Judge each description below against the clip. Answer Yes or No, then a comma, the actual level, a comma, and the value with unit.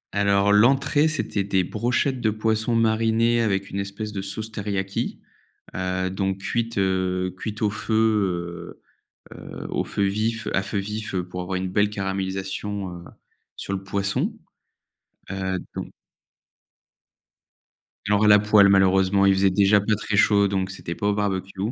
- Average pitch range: No, narrow, 2.0 semitones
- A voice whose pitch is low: Yes, low, 100 Hz